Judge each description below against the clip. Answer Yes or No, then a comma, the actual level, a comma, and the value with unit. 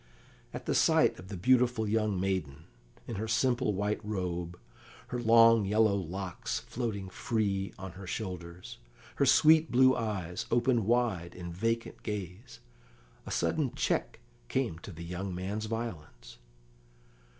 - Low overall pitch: Yes, low, 105 Hz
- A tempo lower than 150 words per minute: Yes, average, 140 wpm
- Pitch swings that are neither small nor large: Yes, average, 4.0 semitones